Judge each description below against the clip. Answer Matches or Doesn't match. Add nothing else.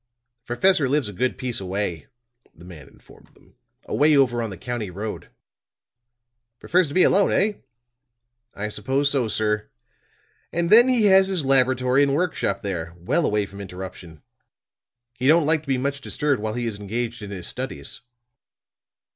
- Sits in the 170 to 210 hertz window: Doesn't match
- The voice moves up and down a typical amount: Doesn't match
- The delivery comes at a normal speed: Matches